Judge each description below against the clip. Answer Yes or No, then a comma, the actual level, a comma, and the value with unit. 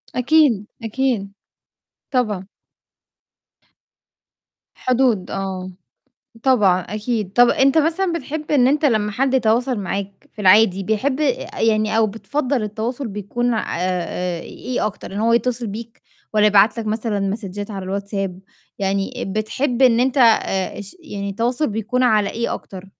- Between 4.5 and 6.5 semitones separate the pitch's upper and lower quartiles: No, average, 4.1 semitones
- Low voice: No, high, 220 Hz